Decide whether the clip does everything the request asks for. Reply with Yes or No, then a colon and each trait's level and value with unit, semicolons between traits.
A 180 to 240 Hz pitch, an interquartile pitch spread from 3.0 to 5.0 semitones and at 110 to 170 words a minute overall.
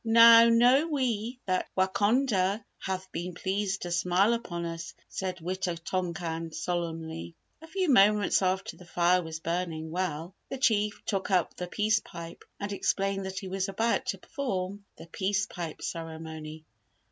Yes: high, 190 Hz; average, 3.5 semitones; average, 155 wpm